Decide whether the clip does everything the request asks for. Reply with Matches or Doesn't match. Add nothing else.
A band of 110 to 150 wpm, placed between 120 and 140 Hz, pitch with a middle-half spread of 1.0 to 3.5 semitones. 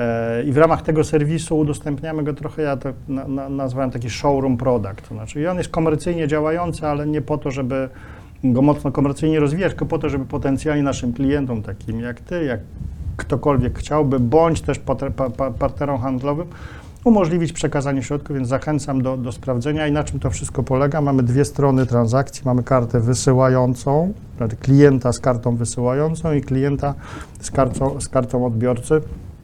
Doesn't match